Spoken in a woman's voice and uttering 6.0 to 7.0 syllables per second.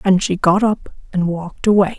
No: female; 5.2 syllables/s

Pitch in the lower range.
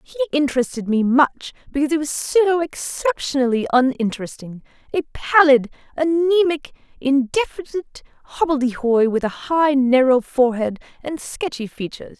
No: very high, 280 Hz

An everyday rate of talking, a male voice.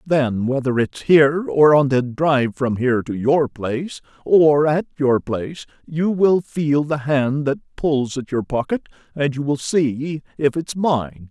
Yes: average, 180 wpm; male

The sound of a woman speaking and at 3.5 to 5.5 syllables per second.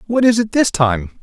No: male; 4.7 syllables/s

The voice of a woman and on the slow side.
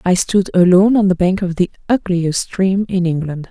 No: female; fast, 205 wpm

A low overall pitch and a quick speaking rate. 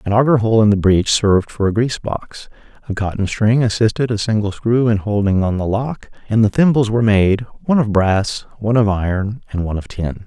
Yes: low, 105 Hz; fast, 220 wpm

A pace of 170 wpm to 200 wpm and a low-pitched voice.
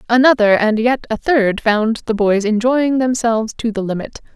No: average, 180 wpm; high, 230 Hz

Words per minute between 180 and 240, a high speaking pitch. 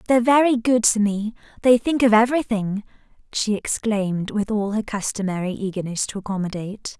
No: average, 145 wpm; high, 215 Hz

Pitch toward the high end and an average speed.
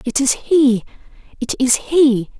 Yes: very high, 260 Hz; average, 150 wpm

